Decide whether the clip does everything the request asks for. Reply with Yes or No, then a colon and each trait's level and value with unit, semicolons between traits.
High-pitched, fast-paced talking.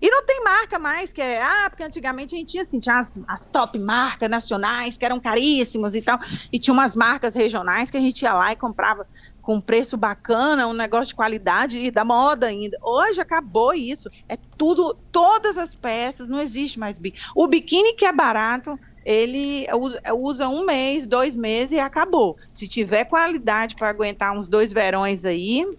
Yes: high, 245 Hz; fast, 190 wpm